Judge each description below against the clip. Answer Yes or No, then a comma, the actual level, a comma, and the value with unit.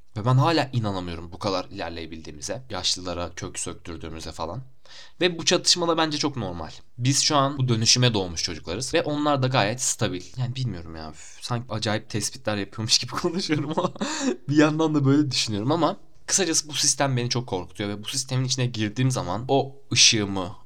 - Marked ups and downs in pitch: Yes, wide, 6.7 semitones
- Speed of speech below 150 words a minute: No, fast, 175 wpm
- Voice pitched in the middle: No, low, 125 Hz